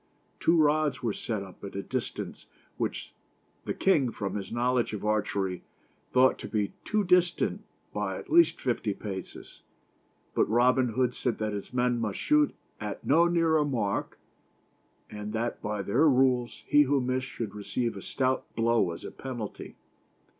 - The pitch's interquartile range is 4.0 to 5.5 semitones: Yes, average, 4.4 semitones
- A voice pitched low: Yes, low, 120 Hz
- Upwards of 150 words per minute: Yes, average, 160 wpm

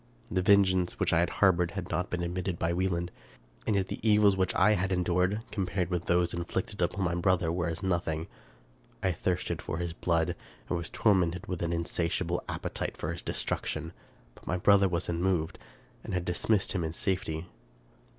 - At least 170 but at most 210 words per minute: Yes, average, 185 wpm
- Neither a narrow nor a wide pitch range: No, narrow, 1.7 semitones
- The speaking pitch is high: No, very low, 90 Hz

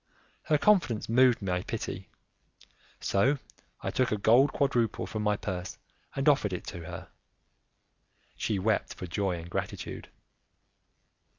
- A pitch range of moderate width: No, wide, 5.7 semitones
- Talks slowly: Yes, slow, 130 wpm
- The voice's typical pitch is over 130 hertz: No, low, 110 Hz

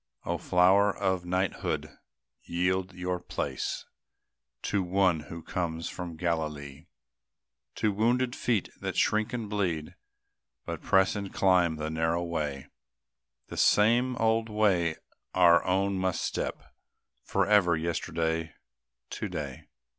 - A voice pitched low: Yes, very low, 90 Hz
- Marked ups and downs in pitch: No, average, 3.3 semitones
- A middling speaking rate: No, slow, 115 wpm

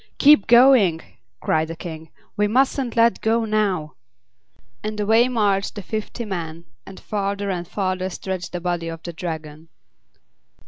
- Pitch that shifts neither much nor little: Yes, average, 4.3 semitones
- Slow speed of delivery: No, average, 145 wpm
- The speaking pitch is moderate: No, high, 195 Hz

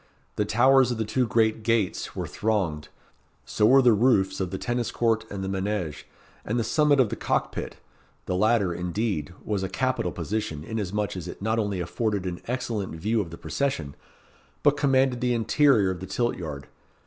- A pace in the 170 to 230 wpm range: Yes, average, 190 wpm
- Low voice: Yes, low, 105 Hz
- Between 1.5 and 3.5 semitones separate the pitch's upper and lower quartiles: No, average, 4.2 semitones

